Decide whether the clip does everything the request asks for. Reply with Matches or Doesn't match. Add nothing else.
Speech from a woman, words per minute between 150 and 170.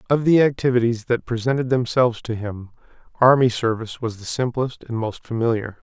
Doesn't match